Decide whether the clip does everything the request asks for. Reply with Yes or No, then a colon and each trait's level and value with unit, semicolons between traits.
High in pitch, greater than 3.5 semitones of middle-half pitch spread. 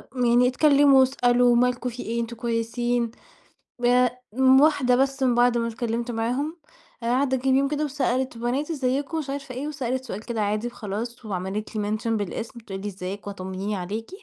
No: high, 245 Hz; average, 2.7 semitones